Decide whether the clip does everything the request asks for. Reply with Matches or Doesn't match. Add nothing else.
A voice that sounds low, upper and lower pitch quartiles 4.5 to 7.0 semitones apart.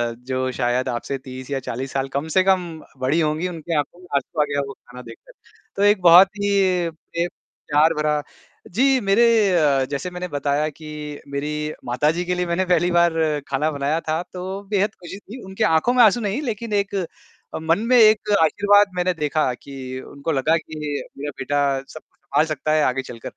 Doesn't match